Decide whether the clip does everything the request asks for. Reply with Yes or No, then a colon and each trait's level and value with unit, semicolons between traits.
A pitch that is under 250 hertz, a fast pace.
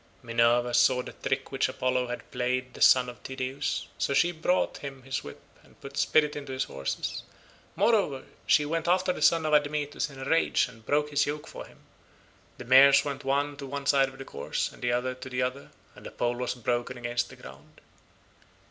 Yes: low, 135 Hz; fast, 210 wpm